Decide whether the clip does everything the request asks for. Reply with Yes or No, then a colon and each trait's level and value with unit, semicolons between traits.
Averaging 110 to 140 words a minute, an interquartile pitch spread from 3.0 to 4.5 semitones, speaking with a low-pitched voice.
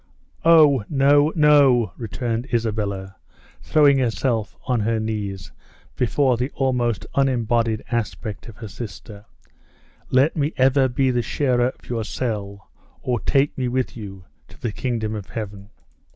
Yes: slow, 135 wpm; average, 3.7 semitones; low, 120 Hz